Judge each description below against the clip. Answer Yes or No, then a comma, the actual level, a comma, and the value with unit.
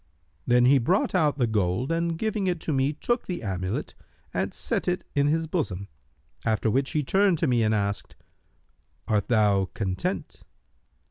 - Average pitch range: No, wide, 7.8 semitones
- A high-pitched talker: No, low, 135 Hz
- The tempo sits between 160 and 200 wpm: Yes, average, 165 wpm